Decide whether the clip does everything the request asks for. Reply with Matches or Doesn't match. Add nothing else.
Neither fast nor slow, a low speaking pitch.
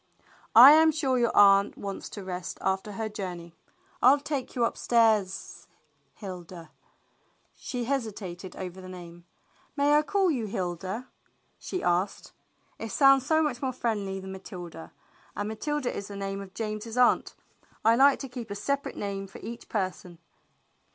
Doesn't match